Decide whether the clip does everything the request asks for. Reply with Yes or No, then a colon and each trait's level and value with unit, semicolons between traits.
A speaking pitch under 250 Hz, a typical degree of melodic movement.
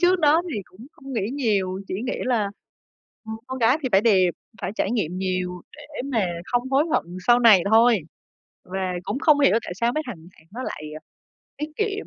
No: high, 235 Hz; wide, 6.0 semitones